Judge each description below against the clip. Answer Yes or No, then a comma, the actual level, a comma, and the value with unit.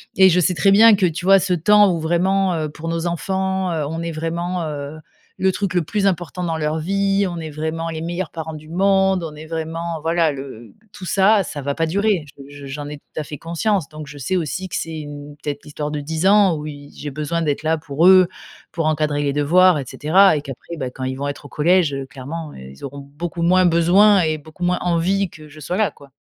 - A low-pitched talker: No, medium, 165 Hz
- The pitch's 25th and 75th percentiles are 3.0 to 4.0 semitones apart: Yes, average, 3.6 semitones